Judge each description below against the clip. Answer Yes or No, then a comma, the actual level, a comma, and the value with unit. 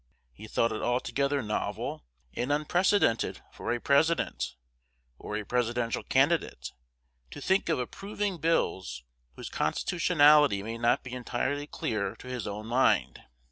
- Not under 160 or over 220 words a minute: No, slow, 135 wpm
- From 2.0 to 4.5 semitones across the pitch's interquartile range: No, average, 5.1 semitones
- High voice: No, low, 125 Hz